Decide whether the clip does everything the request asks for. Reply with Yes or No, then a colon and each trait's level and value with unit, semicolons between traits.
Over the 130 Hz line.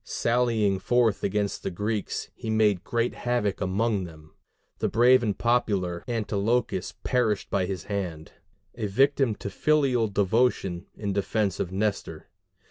No: low, 105 Hz